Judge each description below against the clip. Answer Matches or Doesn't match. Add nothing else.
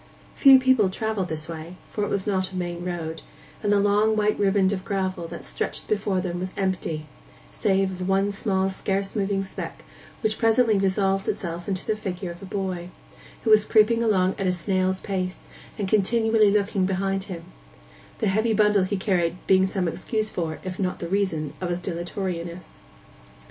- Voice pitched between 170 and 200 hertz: Matches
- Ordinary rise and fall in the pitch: Doesn't match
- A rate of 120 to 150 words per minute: Doesn't match